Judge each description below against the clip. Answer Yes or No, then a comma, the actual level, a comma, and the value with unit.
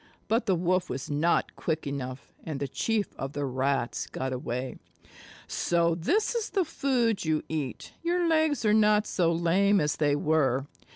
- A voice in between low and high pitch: Yes, medium, 165 Hz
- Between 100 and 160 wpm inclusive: No, average, 170 wpm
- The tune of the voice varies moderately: No, wide, 7.5 semitones